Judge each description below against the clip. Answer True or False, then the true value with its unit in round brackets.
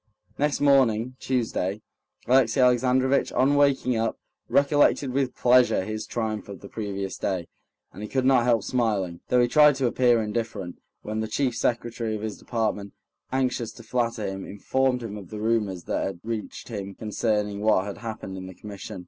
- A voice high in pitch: False (115 Hz)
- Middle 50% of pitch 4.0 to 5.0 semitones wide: False (3.6 semitones)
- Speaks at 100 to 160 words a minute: False (175 wpm)